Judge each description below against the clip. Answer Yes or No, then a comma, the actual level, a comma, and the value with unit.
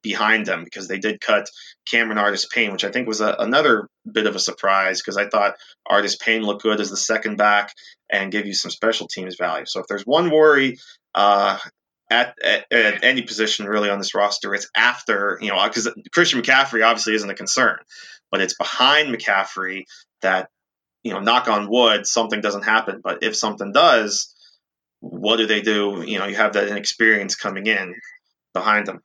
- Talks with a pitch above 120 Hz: No, low, 105 Hz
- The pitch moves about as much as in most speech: No, narrow, 2.0 semitones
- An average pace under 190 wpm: No, average, 195 wpm